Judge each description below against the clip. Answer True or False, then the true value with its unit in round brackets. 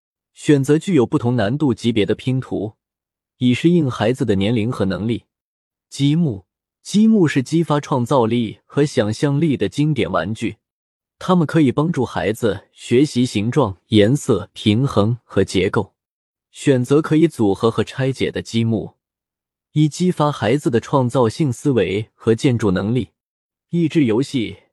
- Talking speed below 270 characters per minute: True (230 characters per minute)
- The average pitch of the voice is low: True (130 Hz)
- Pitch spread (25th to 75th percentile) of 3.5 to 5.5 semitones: True (5.2 semitones)